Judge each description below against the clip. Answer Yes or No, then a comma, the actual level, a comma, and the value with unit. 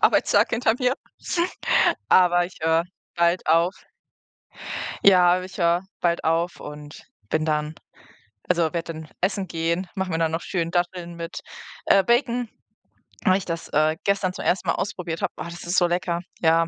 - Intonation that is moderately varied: No, narrow, 2.0 semitones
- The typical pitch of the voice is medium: Yes, medium, 175 Hz